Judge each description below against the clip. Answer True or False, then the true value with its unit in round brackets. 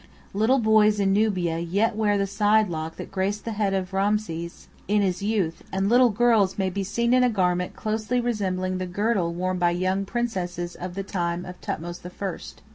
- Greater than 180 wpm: True (200 wpm)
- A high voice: True (195 Hz)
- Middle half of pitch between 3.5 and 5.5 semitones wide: False (3.0 semitones)